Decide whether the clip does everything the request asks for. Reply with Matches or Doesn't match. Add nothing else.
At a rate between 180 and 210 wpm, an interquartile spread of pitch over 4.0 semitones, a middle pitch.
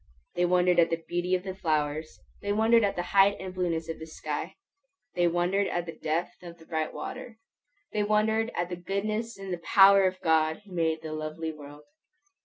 Doesn't match